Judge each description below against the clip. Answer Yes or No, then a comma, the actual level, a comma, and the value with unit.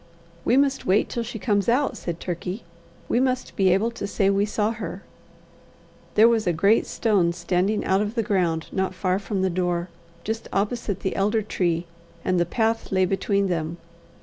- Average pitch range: Yes, average, 3.5 semitones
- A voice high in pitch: Yes, high, 200 Hz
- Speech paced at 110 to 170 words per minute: No, average, 185 wpm